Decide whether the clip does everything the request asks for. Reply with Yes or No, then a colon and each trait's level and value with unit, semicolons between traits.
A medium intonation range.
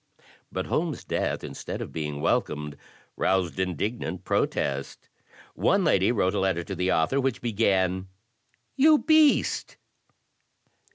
No: wide, 5.9 semitones